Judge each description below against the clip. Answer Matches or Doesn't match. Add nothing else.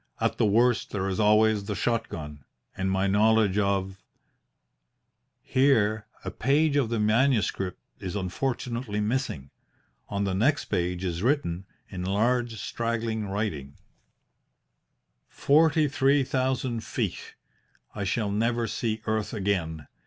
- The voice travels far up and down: Doesn't match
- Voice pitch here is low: Matches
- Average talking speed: Doesn't match